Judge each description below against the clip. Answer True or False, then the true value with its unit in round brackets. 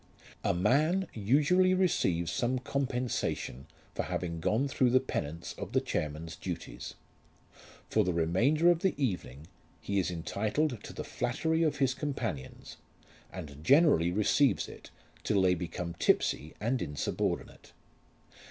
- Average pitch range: False (8.7 semitones)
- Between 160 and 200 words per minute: False (135 wpm)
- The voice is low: True (110 Hz)